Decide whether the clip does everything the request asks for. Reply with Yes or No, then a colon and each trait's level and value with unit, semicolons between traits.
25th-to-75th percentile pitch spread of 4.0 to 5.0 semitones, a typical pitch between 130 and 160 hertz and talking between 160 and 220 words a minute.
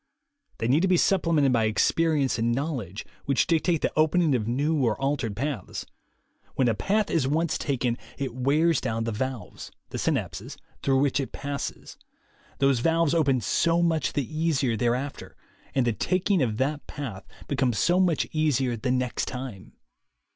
Yes: average, 4.7 semitones; low, 135 Hz; average, 165 wpm